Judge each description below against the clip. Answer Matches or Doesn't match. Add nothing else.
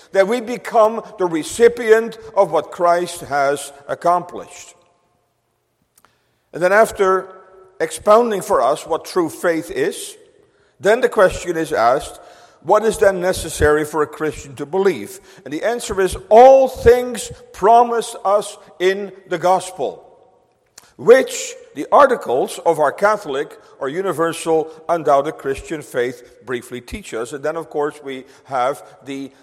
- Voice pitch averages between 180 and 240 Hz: Matches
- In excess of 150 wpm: Doesn't match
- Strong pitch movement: Matches